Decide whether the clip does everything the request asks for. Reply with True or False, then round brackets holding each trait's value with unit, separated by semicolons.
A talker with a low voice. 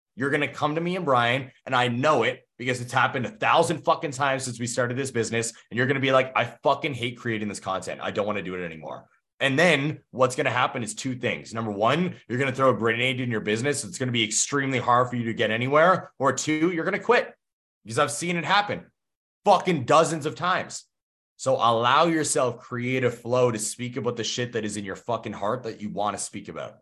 True (125 Hz)